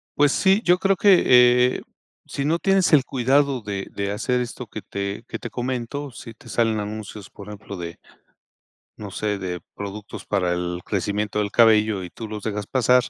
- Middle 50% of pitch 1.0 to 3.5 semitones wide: No, average, 4.0 semitones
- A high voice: No, low, 110 Hz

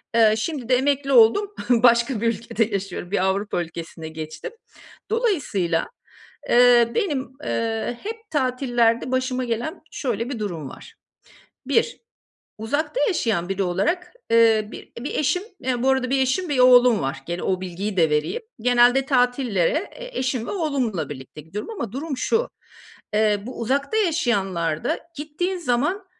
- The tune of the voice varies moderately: No, wide, 5.7 semitones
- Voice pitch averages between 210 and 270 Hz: Yes, high, 240 Hz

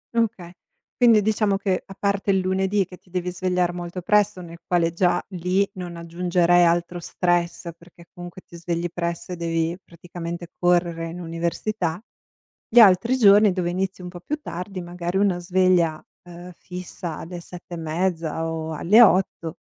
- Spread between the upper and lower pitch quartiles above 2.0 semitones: No, narrow, 1.7 semitones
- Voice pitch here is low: No, medium, 175 Hz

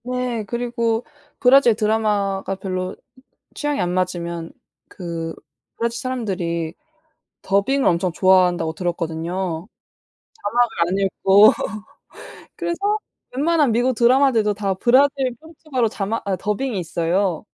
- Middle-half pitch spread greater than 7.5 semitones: No, wide, 5.5 semitones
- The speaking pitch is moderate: No, high, 205 Hz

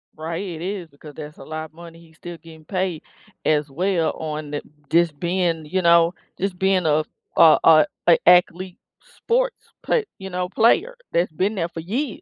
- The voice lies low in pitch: No, medium, 170 Hz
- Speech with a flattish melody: No, average, 3.0 semitones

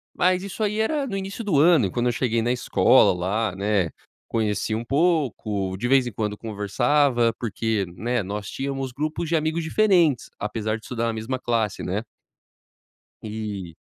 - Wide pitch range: Yes, wide, 6.4 semitones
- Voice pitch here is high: No, low, 120 Hz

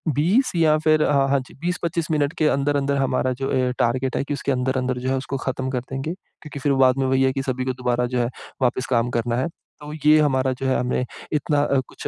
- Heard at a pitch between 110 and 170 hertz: Yes, low, 135 Hz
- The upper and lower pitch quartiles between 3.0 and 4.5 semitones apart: No, narrow, 2.4 semitones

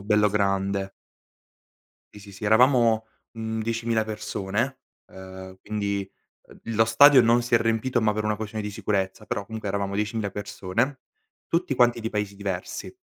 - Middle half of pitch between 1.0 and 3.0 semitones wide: Yes, narrow, 2.4 semitones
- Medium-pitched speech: No, low, 105 Hz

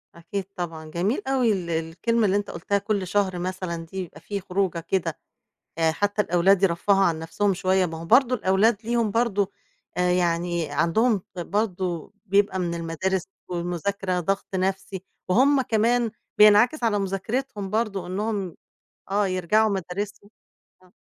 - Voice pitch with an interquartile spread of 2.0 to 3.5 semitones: Yes, average, 3.0 semitones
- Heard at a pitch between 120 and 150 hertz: No, high, 190 Hz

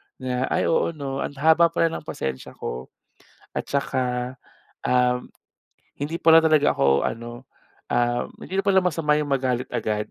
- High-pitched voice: No, low, 135 Hz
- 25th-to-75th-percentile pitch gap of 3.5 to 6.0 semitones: Yes, average, 4.6 semitones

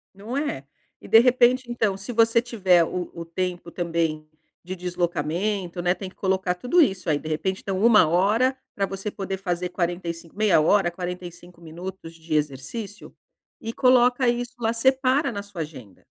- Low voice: No, high, 190 Hz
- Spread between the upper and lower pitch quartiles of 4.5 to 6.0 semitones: Yes, average, 4.8 semitones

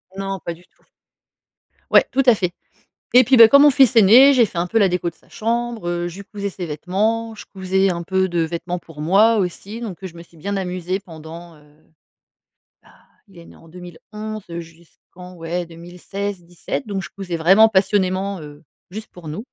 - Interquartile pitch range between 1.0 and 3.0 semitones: No, average, 3.6 semitones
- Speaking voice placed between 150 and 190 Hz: Yes, medium, 185 Hz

